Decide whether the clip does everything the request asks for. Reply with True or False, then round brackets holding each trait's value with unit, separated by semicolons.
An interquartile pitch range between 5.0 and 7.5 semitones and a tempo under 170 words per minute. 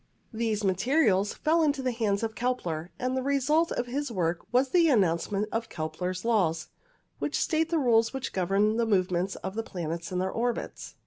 False (5.6 semitones; 185 wpm)